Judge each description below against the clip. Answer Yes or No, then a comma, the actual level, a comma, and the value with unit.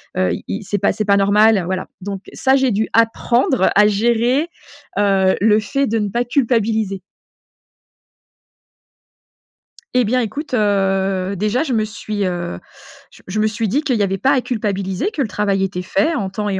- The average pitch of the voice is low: No, high, 210 Hz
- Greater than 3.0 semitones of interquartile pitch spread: Yes, average, 3.4 semitones